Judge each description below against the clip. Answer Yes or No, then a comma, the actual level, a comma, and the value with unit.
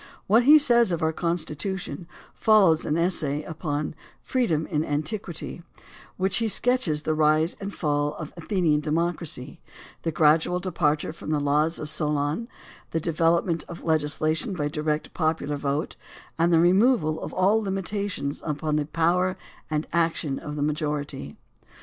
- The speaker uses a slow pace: No, average, 155 wpm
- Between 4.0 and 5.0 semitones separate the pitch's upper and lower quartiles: No, average, 3.3 semitones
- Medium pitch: Yes, medium, 160 Hz